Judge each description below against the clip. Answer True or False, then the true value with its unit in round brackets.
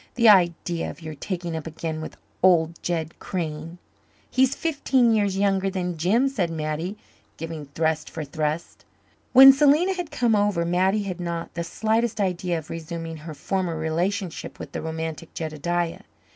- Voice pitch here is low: False (175 Hz)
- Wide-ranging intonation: False (4.0 semitones)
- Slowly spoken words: False (160 wpm)